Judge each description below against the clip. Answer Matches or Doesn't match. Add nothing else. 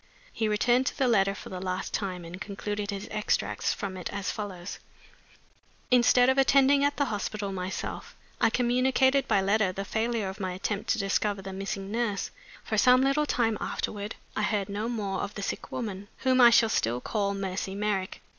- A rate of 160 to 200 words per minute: Matches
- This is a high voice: Matches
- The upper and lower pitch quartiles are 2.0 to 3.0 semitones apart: Doesn't match